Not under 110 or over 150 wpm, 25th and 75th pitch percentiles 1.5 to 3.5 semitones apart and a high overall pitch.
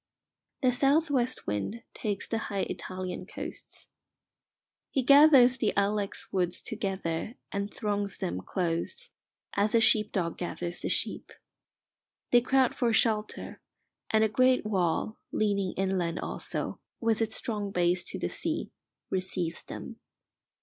No: slow, 135 wpm; average, 4.2 semitones; high, 205 Hz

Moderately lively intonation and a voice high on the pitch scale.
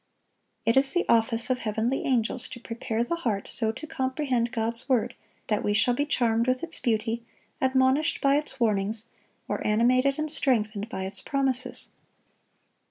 Yes: average, 3.0 semitones; high, 240 Hz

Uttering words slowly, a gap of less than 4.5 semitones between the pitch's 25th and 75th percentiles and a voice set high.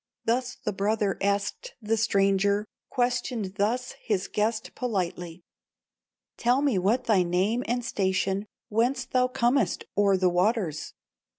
Yes: slow, 125 wpm; average, 3.9 semitones; high, 210 Hz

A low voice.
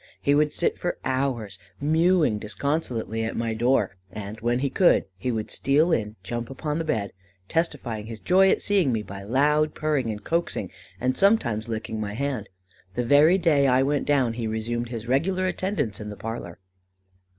Yes: low, 125 Hz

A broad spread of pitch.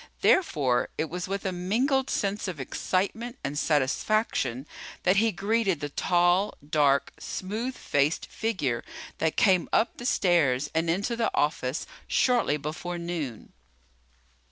Yes: wide, 6.3 semitones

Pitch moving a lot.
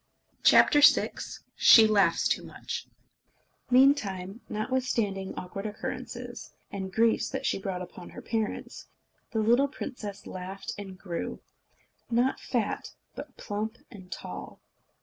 No: average, 3.8 semitones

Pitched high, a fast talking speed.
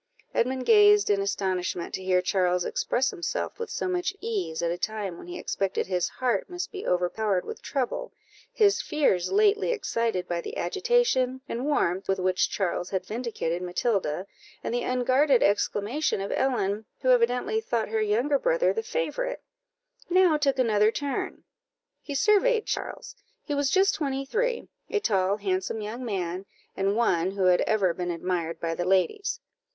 No: high, 230 Hz; average, 165 wpm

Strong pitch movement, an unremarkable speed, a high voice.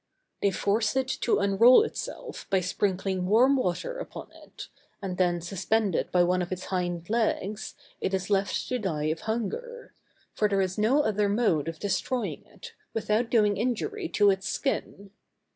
No: average, 4.2 semitones; average, 170 wpm; high, 205 Hz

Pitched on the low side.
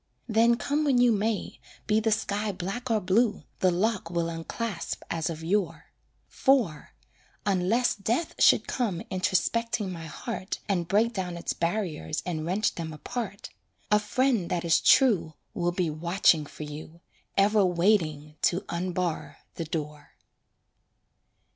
No: medium, 185 Hz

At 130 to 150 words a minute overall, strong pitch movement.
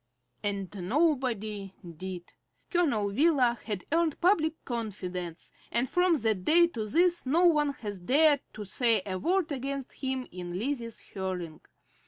Yes: average, 140 wpm; wide, 7.7 semitones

